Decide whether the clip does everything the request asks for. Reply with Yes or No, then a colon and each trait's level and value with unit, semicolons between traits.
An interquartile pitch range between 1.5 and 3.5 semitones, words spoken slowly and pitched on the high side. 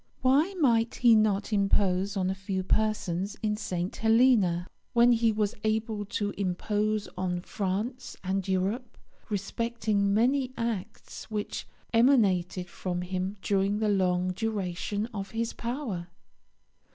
Yes: average, 3.2 semitones; slow, 125 wpm; high, 205 Hz